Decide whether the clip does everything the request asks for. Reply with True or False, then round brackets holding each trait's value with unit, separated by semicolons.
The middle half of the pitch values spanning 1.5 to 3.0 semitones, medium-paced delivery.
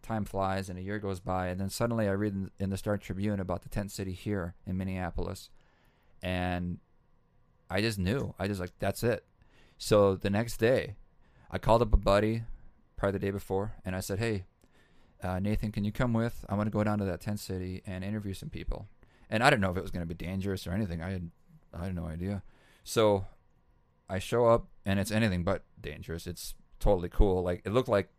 False (2.4 semitones; 215 wpm)